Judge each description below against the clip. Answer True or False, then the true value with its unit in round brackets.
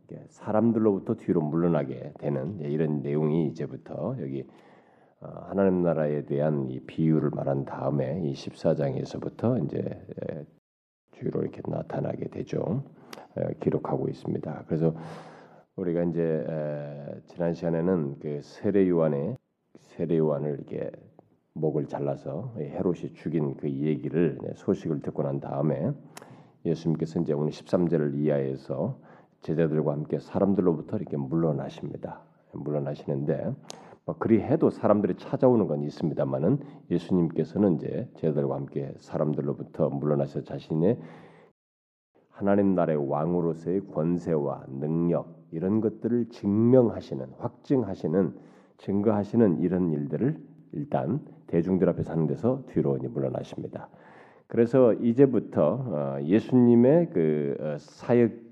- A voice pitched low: True (80 Hz)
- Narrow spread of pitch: False (4.8 semitones)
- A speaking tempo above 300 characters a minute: False (295 characters per minute)